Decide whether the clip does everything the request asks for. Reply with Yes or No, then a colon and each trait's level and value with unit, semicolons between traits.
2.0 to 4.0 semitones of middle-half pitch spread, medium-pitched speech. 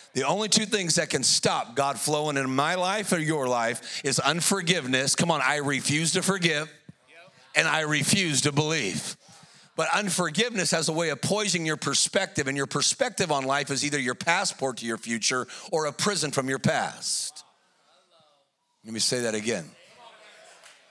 No: average, 4.7 semitones; medium, 150 Hz